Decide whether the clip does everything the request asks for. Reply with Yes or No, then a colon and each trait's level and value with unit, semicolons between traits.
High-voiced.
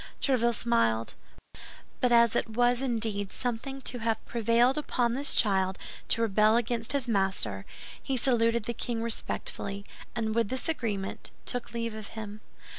Yes: high, 230 Hz